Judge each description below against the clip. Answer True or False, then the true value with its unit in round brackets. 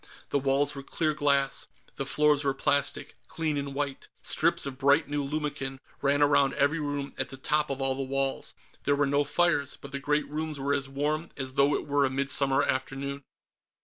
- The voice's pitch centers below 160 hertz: True (140 Hz)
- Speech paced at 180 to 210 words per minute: True (200 wpm)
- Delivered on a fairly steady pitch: True (1.1 semitones)